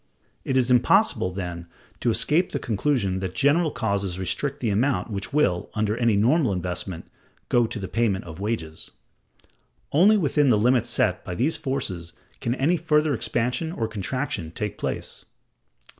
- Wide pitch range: Yes, wide, 6.8 semitones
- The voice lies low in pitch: Yes, low, 115 Hz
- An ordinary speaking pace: Yes, average, 160 wpm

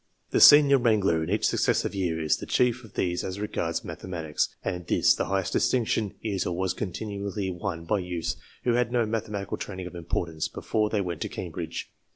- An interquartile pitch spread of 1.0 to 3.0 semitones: No, average, 3.7 semitones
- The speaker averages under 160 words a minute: No, average, 195 wpm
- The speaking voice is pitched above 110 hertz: No, very low, 95 Hz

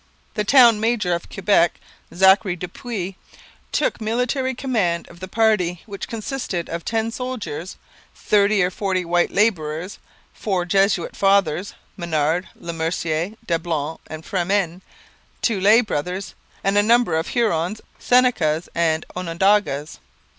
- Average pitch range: Yes, average, 4.2 semitones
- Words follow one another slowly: Yes, slow, 130 wpm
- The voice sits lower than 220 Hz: Yes, high, 190 Hz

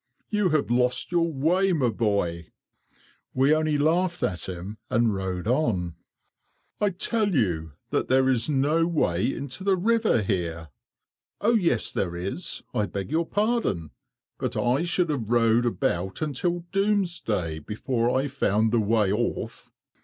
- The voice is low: Yes, low, 125 Hz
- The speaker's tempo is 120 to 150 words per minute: Yes, average, 145 wpm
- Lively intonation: Yes, wide, 8.8 semitones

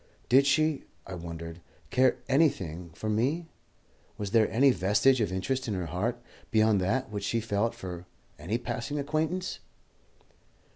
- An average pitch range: No, wide, 6.1 semitones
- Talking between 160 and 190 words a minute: No, average, 145 wpm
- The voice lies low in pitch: Yes, low, 115 Hz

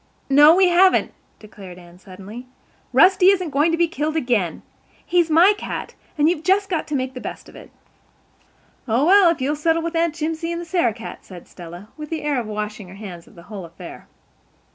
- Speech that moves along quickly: Yes, fast, 210 wpm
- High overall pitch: Yes, very high, 295 Hz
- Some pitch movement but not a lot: No, wide, 8.1 semitones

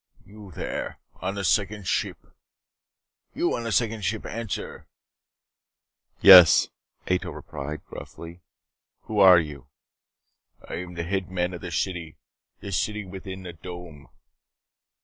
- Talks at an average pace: No, slow, 130 wpm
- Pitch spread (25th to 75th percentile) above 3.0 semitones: No, average, 2.7 semitones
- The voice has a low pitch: Yes, very low, 90 Hz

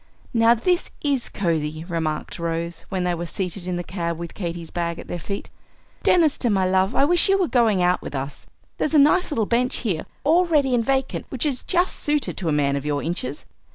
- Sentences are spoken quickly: Yes, fast, 220 wpm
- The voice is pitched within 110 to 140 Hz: No, high, 190 Hz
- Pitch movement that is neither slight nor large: No, wide, 8.2 semitones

